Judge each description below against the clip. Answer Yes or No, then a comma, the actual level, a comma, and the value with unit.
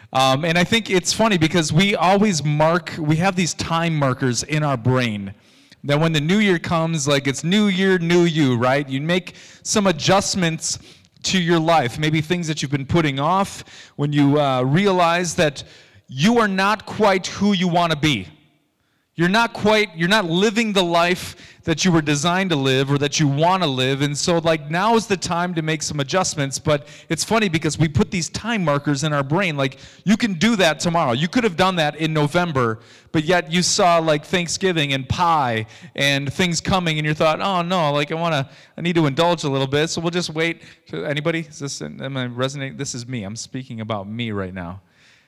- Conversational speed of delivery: No, fast, 215 wpm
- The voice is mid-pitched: Yes, medium, 160 Hz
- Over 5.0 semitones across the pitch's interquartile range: No, average, 4.3 semitones